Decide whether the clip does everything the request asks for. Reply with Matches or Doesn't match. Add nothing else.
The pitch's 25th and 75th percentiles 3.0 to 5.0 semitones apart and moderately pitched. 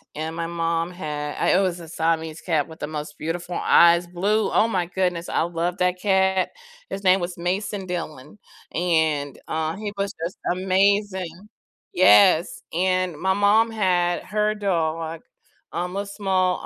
Doesn't match